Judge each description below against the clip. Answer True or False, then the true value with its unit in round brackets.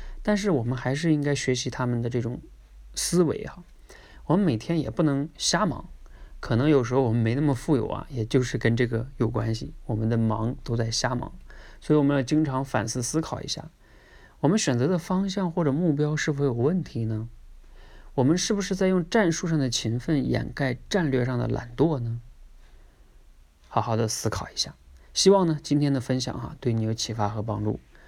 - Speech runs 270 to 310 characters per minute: True (290 characters per minute)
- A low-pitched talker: True (130 Hz)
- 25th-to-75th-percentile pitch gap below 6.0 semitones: True (5.2 semitones)